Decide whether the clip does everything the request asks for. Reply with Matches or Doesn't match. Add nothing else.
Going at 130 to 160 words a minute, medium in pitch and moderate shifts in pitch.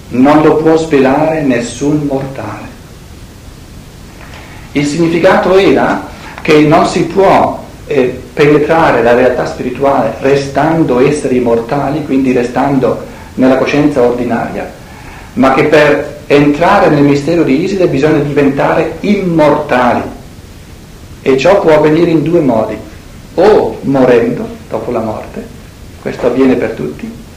Doesn't match